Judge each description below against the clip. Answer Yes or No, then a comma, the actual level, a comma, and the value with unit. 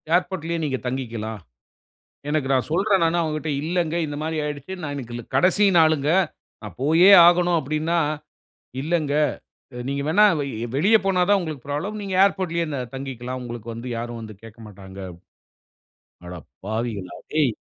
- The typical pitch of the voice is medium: Yes, medium, 150 Hz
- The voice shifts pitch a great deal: Yes, wide, 6.3 semitones